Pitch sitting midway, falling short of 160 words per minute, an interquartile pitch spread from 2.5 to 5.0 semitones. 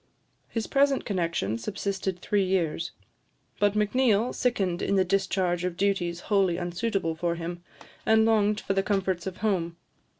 No: high, 195 Hz; average, 145 wpm; average, 3.0 semitones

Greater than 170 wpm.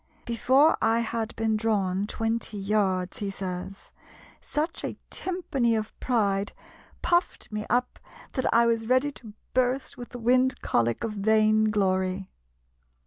No: average, 140 wpm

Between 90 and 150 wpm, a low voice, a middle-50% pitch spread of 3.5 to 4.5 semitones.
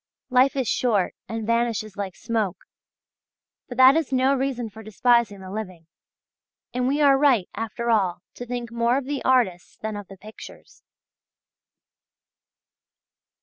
No: average, 145 wpm; high, 235 Hz; average, 3.8 semitones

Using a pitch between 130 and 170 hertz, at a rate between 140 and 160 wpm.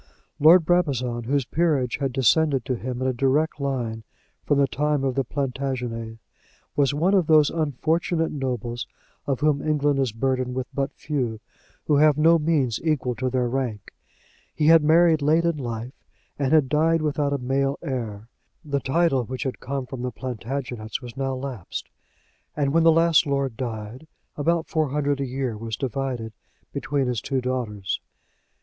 No: low, 135 Hz; average, 170 wpm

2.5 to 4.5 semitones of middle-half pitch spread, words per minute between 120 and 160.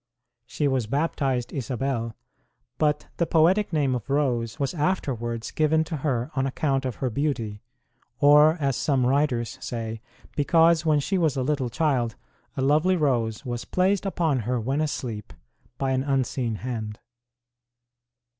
Yes: average, 4.1 semitones; average, 145 wpm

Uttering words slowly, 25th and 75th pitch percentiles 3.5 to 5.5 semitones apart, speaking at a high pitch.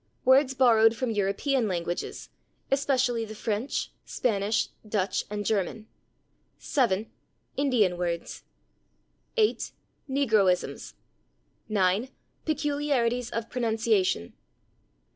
Yes: slow, 85 wpm; average, 4.5 semitones; high, 225 Hz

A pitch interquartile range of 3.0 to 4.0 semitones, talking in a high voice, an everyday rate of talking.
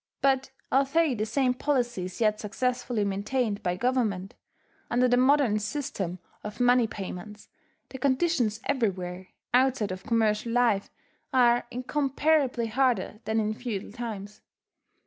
No: average, 3.7 semitones; high, 235 Hz; slow, 125 wpm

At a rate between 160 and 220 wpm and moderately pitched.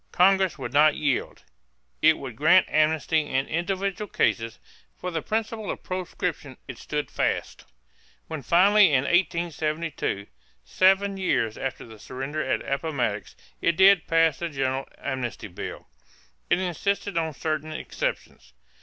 No: slow, 135 wpm; medium, 160 Hz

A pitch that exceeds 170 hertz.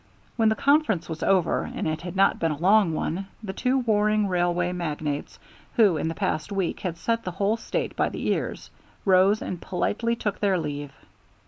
Yes: medium, 185 Hz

